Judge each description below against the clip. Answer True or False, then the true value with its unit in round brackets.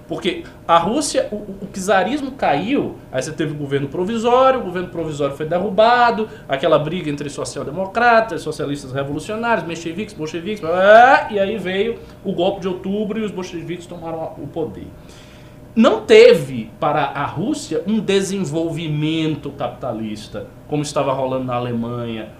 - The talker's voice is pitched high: False (170 Hz)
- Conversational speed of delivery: True (140 wpm)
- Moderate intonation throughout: False (6.3 semitones)